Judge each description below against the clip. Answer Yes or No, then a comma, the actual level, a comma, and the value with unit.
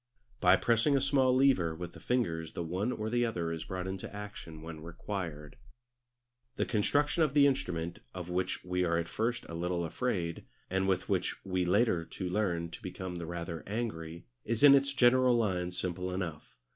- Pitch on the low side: Yes, very low, 95 Hz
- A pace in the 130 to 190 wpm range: Yes, average, 185 wpm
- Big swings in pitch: Yes, wide, 5.7 semitones